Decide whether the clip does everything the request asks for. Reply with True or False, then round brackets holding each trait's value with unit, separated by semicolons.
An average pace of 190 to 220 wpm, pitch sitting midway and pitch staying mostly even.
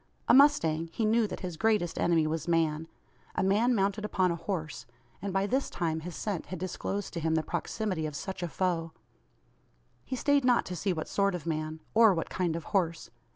False (205 wpm; 180 Hz; 4.1 semitones)